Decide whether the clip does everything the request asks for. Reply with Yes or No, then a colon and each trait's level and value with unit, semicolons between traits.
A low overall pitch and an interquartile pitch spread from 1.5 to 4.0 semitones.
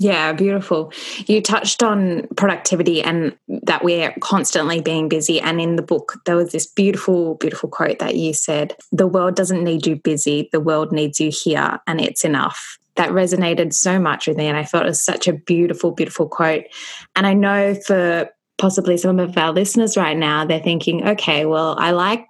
No: medium, 170 Hz; average, 3.2 semitones